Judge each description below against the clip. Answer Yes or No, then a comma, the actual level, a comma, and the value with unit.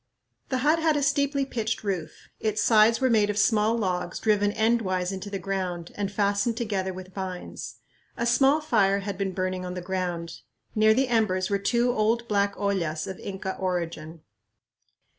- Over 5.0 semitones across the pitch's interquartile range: No, average, 3.6 semitones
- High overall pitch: Yes, high, 200 Hz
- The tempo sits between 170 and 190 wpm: Yes, average, 175 wpm